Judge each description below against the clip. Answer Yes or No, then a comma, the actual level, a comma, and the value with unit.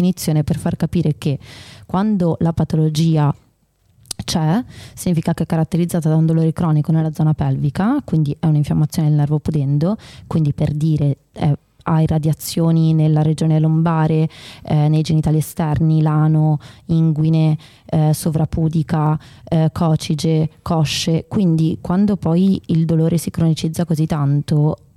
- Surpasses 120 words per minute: Yes, average, 130 wpm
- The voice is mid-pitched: Yes, medium, 160 Hz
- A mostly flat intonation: Yes, narrow, 1.5 semitones